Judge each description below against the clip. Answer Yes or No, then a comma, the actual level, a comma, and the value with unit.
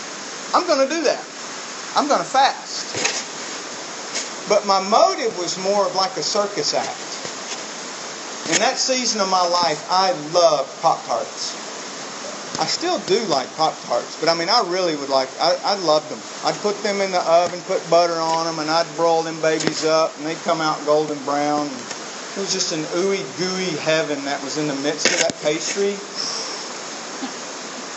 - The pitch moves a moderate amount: Yes, average, 4.0 semitones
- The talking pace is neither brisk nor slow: Yes, average, 170 wpm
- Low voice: No, medium, 170 Hz